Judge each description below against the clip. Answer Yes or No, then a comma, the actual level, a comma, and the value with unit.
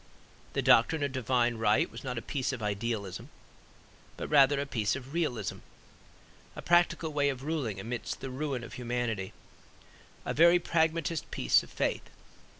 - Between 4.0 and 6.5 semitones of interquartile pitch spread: Yes, average, 4.5 semitones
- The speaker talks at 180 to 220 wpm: No, average, 155 wpm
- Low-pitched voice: Yes, low, 130 Hz